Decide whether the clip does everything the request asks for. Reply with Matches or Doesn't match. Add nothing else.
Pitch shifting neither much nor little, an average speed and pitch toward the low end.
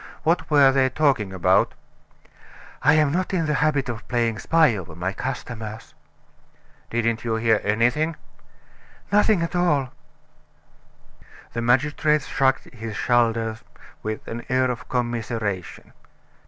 Doesn't match